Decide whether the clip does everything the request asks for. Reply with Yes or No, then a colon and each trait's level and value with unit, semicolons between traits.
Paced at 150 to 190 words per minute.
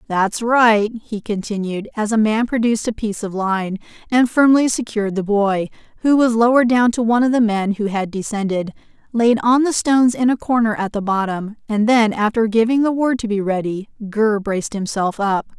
No: average, 200 wpm